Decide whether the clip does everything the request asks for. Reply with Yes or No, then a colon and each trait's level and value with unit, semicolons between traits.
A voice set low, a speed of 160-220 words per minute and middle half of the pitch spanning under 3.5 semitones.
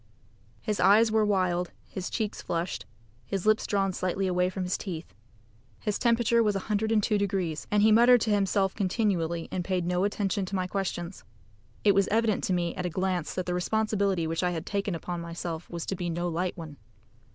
No: high, 190 Hz; average, 195 wpm; average, 2.9 semitones